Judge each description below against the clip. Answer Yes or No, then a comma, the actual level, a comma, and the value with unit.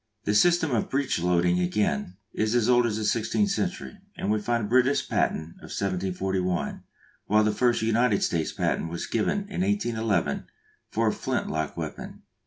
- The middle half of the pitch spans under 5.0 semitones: No, wide, 5.4 semitones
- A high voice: No, low, 110 Hz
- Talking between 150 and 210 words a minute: Yes, average, 175 wpm